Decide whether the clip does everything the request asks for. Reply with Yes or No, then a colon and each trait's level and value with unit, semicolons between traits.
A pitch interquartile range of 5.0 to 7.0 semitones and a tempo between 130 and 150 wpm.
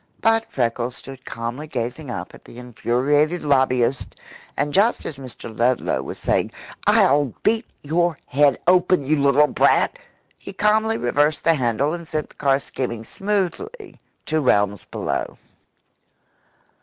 Yes: wide, 5.4 semitones; average, 140 wpm